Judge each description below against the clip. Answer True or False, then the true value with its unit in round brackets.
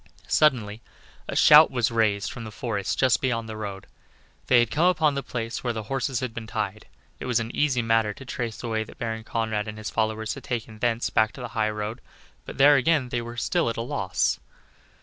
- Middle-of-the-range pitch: False (115 Hz)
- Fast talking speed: True (220 wpm)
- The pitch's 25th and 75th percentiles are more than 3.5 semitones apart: False (2.4 semitones)